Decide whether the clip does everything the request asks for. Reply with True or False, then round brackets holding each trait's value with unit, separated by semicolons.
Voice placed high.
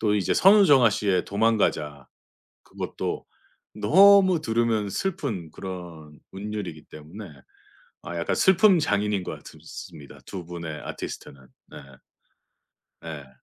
False (100 Hz)